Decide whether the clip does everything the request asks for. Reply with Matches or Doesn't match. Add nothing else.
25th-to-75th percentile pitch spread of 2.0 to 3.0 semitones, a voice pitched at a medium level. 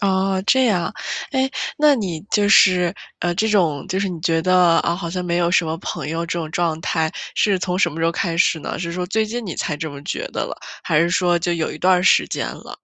Matches